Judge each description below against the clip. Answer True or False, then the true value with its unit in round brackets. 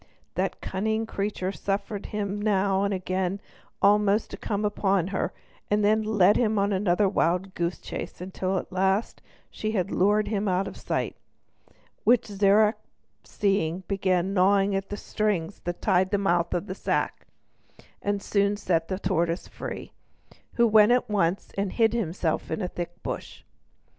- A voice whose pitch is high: True (200 Hz)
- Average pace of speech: True (160 wpm)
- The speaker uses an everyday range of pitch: False (2.1 semitones)